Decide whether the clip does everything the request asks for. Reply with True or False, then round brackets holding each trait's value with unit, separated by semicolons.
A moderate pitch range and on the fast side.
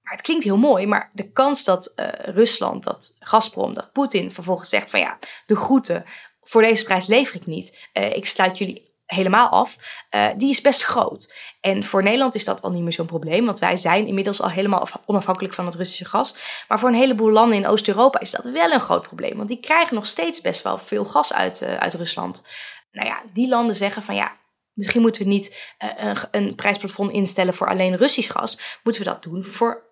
True (3.9 semitones; 220 wpm)